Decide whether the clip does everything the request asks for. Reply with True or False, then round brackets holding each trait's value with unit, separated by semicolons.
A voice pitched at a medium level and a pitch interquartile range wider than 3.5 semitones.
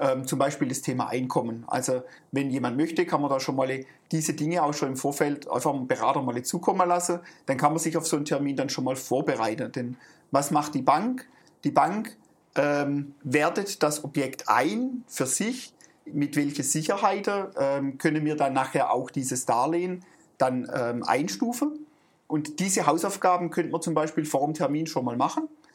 True (150 Hz; 4.7 semitones)